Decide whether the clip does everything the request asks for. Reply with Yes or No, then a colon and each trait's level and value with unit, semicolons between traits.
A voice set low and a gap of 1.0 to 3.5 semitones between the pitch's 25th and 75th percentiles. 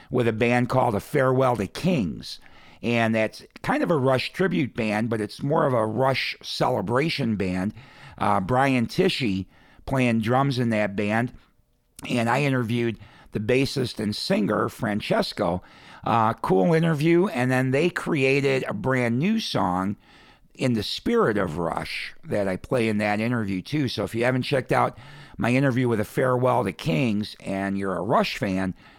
No: low, 125 Hz; average, 4.2 semitones